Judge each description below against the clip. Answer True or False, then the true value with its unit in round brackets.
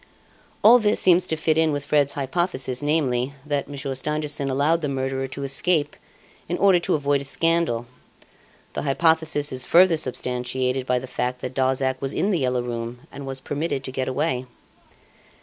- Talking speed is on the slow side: False (175 wpm)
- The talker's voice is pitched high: False (140 Hz)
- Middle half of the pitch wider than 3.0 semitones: True (3.5 semitones)